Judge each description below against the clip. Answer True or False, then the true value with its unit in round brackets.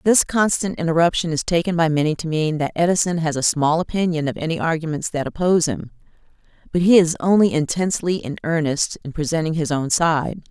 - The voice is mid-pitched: True (165 Hz)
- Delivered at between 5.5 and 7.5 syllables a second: True (5.9 syllables/s)